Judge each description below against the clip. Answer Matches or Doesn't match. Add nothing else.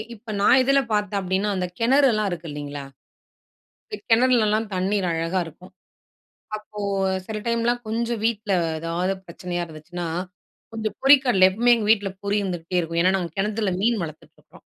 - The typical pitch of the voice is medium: Doesn't match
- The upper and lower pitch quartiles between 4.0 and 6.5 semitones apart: Matches